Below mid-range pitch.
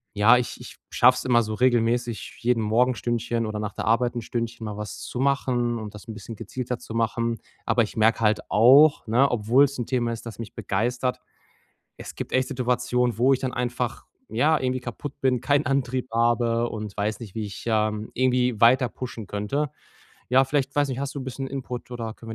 Yes: low, 120 Hz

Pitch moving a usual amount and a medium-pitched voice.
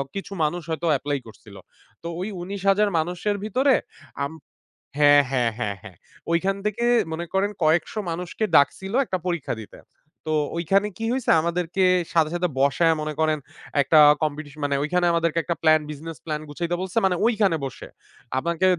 Yes: average, 4.0 semitones; medium, 170 Hz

